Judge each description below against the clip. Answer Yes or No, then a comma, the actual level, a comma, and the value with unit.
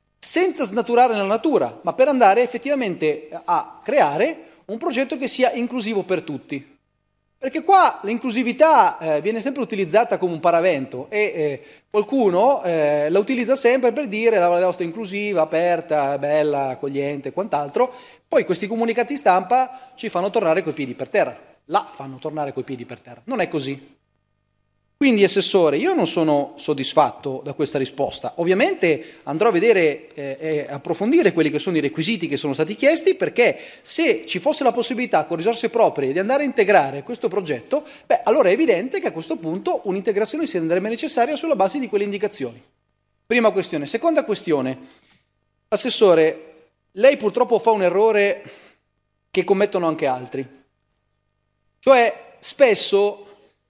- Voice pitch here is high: Yes, high, 195 Hz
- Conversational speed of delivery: Yes, average, 150 wpm